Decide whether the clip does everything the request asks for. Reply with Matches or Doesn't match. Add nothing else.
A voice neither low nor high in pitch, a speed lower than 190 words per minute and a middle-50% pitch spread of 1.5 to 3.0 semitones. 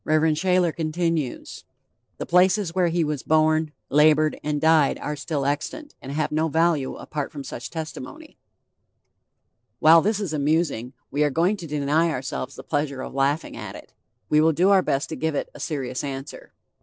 Matches